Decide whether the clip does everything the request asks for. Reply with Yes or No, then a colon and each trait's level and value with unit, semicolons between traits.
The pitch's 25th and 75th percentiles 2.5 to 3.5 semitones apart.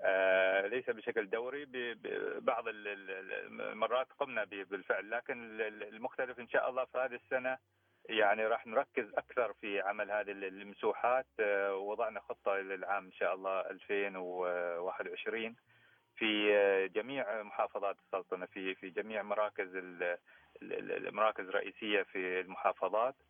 Yes: average, 3.2 semitones